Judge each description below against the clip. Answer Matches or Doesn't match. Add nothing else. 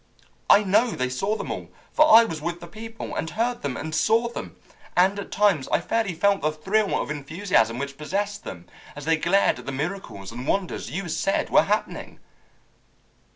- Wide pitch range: Matches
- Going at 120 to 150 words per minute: Doesn't match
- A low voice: Doesn't match